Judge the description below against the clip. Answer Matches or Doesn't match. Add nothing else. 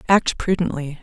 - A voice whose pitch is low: Doesn't match